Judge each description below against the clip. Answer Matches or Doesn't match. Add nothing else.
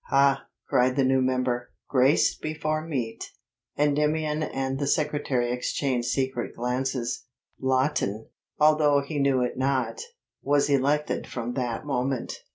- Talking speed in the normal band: Doesn't match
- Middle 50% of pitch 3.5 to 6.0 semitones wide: Doesn't match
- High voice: Doesn't match